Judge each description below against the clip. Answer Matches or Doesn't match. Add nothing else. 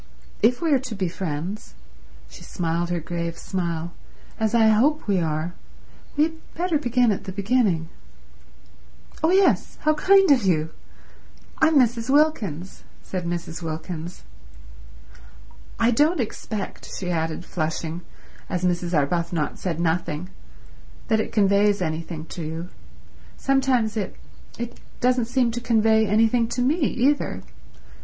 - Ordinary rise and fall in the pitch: Doesn't match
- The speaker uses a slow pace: Matches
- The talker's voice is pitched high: Matches